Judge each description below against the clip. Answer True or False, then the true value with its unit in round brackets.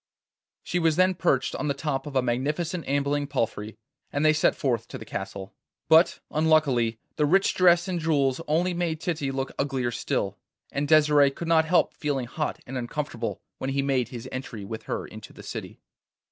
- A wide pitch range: False (3.7 semitones)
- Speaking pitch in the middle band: True (145 Hz)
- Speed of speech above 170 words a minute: True (190 wpm)